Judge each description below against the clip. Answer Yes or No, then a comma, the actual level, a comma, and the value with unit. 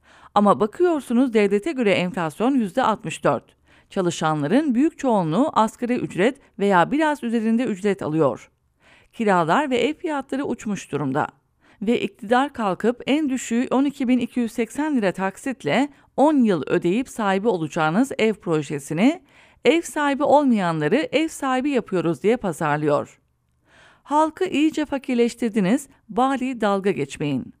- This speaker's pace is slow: Yes, slow, 110 wpm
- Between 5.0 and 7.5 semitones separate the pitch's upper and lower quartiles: Yes, wide, 5.6 semitones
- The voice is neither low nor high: No, high, 235 Hz